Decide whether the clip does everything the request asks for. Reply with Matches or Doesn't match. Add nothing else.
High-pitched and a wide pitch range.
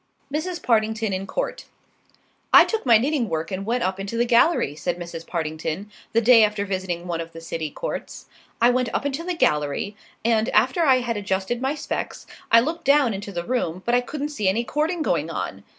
Matches